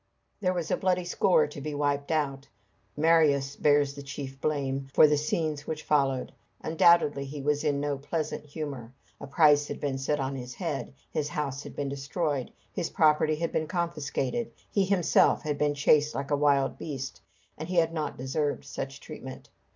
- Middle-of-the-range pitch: Yes, medium, 145 Hz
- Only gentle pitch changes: Yes, narrow, 2.1 semitones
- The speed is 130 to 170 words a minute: No, average, 180 wpm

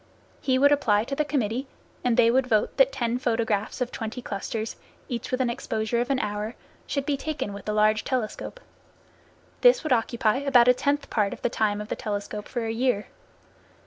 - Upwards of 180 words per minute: Yes, average, 200 wpm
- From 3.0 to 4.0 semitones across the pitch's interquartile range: Yes, average, 3.5 semitones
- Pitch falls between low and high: No, high, 235 Hz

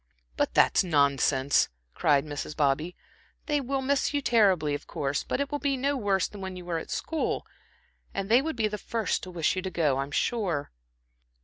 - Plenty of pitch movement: Yes, wide, 9.0 semitones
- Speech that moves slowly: No, fast, 205 wpm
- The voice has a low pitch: No, high, 190 Hz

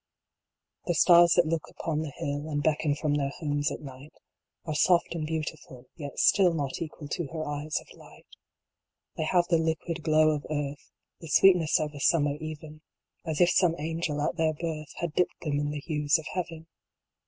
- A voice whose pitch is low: No, medium, 155 Hz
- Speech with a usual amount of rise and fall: No, narrow, 2.1 semitones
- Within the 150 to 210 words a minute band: Yes, average, 190 wpm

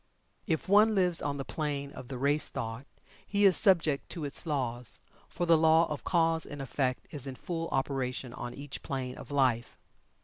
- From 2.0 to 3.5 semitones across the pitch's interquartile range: No, average, 3.9 semitones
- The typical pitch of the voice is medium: Yes, medium, 145 Hz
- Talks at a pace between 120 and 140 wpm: No, average, 190 wpm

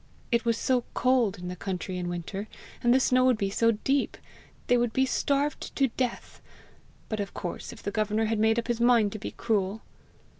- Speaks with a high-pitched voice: Yes, high, 225 Hz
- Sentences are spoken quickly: Yes, fast, 210 wpm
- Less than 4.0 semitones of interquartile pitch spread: Yes, average, 3.4 semitones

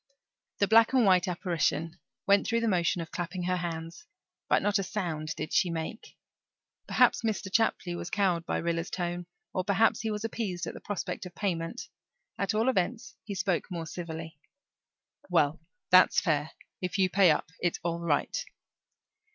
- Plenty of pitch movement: No, average, 3.4 semitones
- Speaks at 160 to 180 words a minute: Yes, average, 170 wpm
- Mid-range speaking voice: Yes, medium, 180 Hz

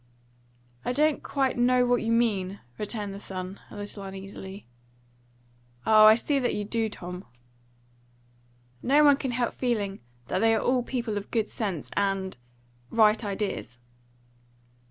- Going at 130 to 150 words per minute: Yes, average, 145 wpm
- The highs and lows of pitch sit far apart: No, average, 3.7 semitones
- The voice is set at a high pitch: Yes, high, 215 Hz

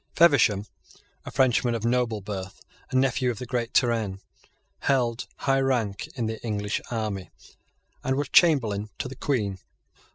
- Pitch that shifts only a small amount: No, average, 3.8 semitones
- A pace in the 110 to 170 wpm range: Yes, average, 150 wpm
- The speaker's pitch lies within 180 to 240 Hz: No, low, 115 Hz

